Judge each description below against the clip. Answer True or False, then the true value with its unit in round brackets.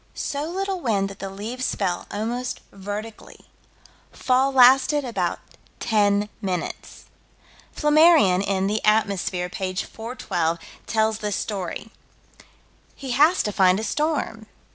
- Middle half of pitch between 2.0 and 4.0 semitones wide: False (4.7 semitones)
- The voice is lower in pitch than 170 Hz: False (220 Hz)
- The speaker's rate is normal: False (120 wpm)